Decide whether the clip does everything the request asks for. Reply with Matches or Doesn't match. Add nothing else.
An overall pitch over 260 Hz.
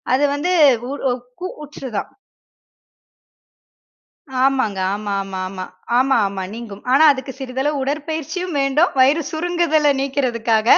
Matches